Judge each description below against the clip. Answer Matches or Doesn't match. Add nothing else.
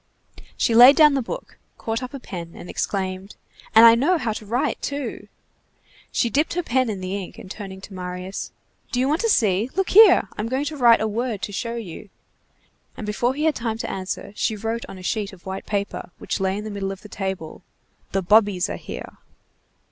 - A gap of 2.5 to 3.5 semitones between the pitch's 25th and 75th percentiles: Doesn't match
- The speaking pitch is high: Matches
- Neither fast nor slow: Doesn't match